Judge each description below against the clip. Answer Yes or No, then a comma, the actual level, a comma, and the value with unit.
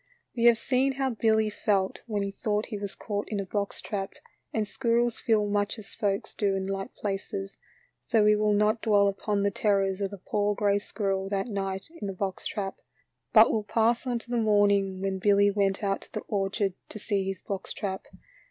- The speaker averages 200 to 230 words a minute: Yes, fast, 205 wpm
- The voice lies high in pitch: Yes, high, 205 Hz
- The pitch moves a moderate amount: No, narrow, 1.6 semitones